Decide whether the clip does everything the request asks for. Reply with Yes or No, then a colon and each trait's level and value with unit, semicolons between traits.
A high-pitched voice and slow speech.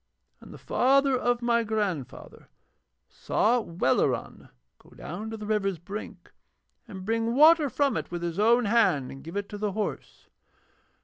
No: high, 215 Hz; average, 160 wpm